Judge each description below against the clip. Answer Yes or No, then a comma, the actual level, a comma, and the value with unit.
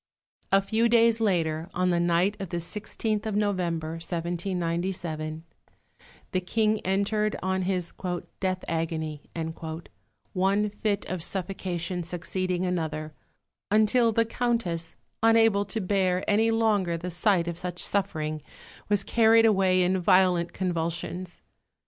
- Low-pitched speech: No, medium, 185 Hz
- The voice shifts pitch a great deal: No, average, 3.3 semitones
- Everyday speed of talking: No, slow, 125 wpm